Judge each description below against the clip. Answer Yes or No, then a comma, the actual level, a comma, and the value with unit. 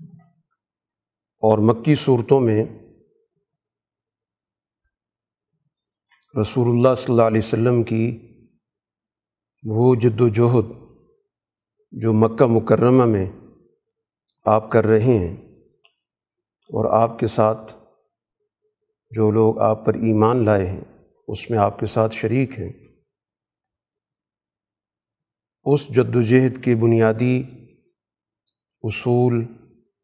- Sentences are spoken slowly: Yes, slow, 95 wpm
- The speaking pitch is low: Yes, low, 115 Hz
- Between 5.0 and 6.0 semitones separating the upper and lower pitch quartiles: No, narrow, 2.6 semitones